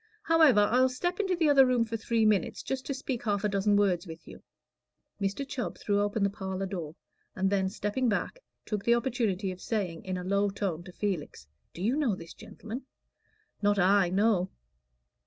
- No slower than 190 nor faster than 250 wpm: Yes, average, 195 wpm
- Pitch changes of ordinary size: Yes, average, 4.2 semitones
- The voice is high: Yes, high, 205 Hz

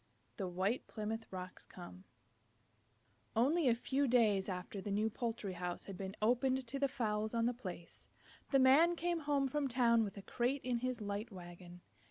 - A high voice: Yes, high, 225 Hz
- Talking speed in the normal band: Yes, average, 180 wpm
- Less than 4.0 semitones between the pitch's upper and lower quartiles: No, average, 5.0 semitones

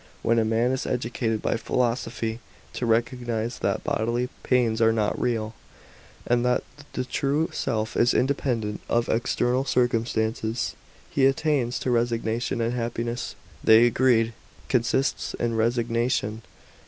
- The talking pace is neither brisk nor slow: No, slow, 130 wpm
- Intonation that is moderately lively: No, narrow, 1.6 semitones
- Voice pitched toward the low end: Yes, low, 120 Hz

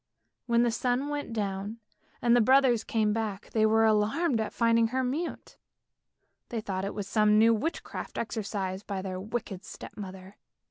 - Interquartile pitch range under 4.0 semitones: Yes, average, 2.9 semitones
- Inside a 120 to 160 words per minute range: No, average, 170 wpm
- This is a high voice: Yes, high, 220 Hz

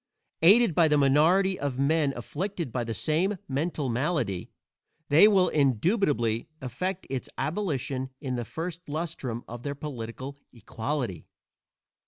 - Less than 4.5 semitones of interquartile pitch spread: No, wide, 5.6 semitones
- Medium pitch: Yes, medium, 145 Hz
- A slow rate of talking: Yes, slow, 130 wpm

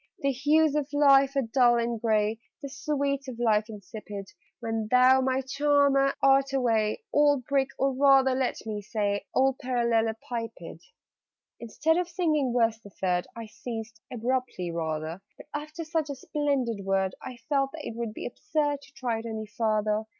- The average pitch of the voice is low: No, very high, 250 Hz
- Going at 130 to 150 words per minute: No, average, 170 wpm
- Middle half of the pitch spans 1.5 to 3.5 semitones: No, average, 4.0 semitones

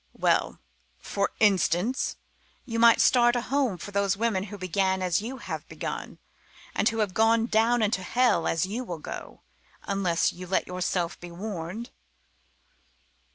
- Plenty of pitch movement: No, average, 4.0 semitones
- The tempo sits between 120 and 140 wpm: No, average, 155 wpm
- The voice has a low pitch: No, high, 200 Hz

